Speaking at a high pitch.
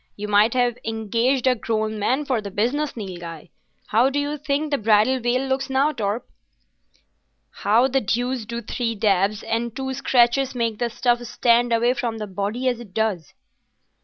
Yes: high, 235 Hz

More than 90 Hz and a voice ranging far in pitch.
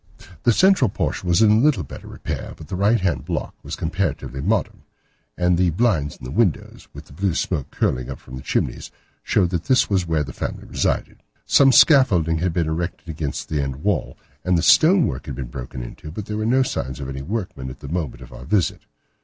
No: very low, 85 Hz; wide, 7.0 semitones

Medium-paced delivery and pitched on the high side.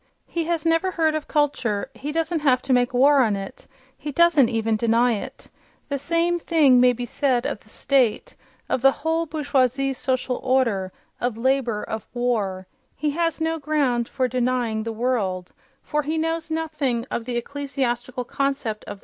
Yes: average, 175 wpm; very high, 260 Hz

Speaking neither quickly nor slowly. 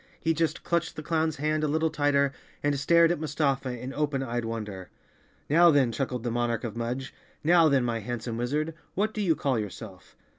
Yes: average, 195 wpm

